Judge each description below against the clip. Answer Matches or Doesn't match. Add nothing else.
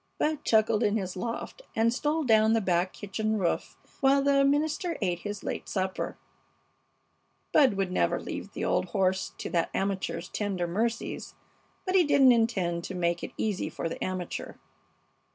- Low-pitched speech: Doesn't match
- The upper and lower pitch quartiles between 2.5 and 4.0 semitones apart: Doesn't match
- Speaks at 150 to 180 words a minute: Matches